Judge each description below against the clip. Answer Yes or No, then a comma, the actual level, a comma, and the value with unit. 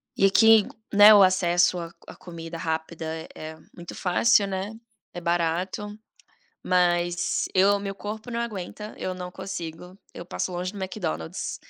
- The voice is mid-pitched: Yes, medium, 180 Hz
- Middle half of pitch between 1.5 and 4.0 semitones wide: Yes, average, 2.7 semitones